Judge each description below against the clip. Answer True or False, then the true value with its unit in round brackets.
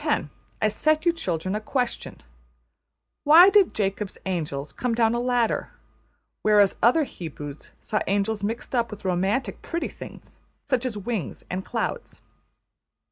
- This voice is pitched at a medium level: False (215 Hz)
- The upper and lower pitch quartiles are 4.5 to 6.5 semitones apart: True (4.8 semitones)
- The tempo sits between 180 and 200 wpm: False (140 wpm)